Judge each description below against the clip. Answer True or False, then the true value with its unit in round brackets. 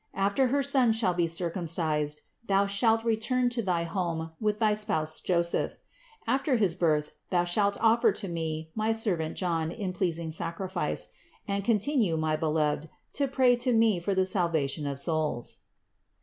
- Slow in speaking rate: False (160 wpm)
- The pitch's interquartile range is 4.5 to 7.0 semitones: True (5.4 semitones)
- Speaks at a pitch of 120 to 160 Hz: False (185 Hz)